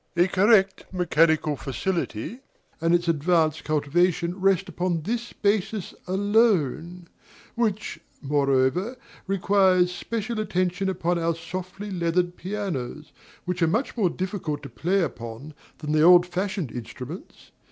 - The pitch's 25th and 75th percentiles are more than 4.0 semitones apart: No, average, 3.6 semitones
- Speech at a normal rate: No, slow, 120 wpm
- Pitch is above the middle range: No, medium, 180 Hz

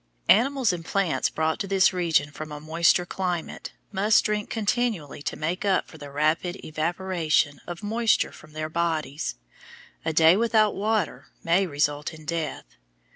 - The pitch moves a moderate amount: Yes, average, 4.3 semitones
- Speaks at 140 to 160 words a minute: Yes, average, 155 wpm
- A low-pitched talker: No, medium, 170 Hz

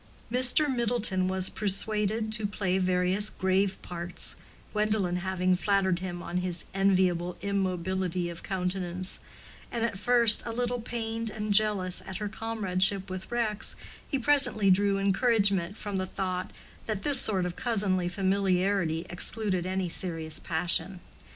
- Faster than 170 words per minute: No, average, 140 wpm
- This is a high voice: Yes, high, 195 Hz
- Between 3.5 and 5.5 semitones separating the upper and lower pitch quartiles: No, average, 2.7 semitones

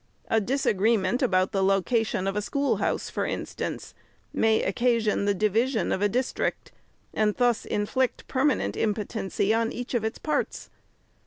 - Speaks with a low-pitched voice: No, high, 220 Hz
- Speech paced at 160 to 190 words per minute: No, average, 145 wpm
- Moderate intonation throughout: Yes, average, 3.3 semitones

